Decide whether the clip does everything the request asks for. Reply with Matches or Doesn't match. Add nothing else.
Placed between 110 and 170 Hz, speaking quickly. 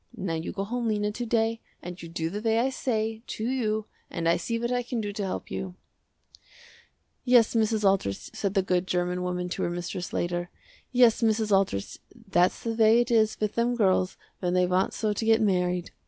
Doesn't match